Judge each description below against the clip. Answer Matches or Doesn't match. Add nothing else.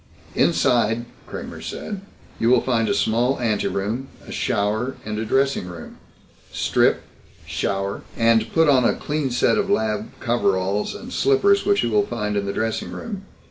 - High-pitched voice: Doesn't match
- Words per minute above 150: Matches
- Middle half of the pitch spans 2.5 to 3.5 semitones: Doesn't match